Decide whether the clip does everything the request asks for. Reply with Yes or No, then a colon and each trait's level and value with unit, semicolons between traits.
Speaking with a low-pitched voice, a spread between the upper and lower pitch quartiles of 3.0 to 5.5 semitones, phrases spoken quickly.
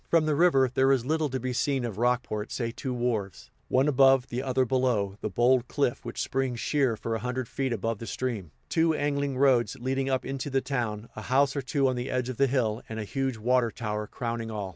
No: low, 125 Hz; narrow, 2.6 semitones; fast, 230 wpm